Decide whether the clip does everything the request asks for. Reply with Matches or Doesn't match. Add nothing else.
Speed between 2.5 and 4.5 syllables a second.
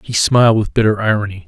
Doesn't match